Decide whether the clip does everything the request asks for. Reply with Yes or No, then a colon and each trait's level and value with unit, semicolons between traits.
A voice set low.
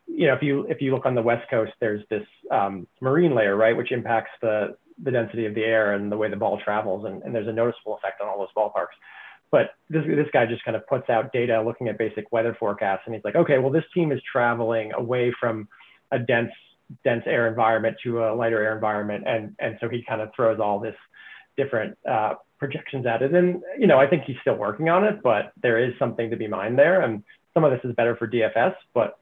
Yes: low, 115 Hz